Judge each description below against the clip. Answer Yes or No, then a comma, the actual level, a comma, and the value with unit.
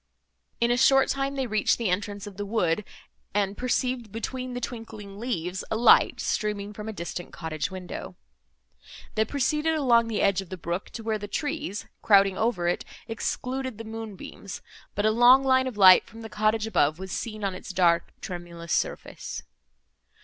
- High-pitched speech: Yes, high, 215 Hz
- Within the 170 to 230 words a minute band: Yes, average, 180 wpm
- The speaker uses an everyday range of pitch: Yes, average, 4.0 semitones